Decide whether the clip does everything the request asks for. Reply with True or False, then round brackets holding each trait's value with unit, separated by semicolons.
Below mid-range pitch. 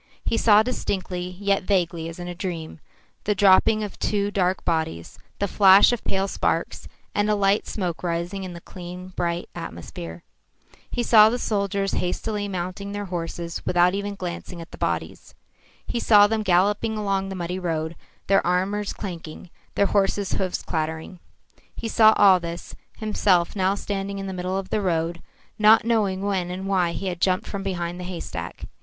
False (190 Hz)